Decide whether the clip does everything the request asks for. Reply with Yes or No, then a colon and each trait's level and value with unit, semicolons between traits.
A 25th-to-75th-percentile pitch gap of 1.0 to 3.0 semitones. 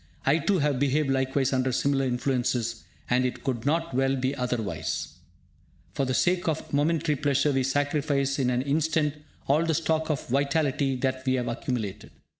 Yes: narrow, 2.6 semitones